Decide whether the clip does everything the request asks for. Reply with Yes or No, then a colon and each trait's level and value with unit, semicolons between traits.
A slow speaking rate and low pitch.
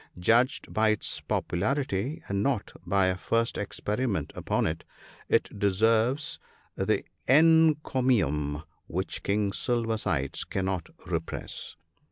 Yes: slow, 110 wpm; low, 110 Hz